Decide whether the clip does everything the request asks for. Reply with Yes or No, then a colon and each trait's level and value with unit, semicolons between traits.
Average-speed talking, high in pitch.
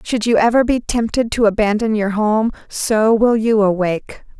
Yes: average, 175 wpm; high, 220 Hz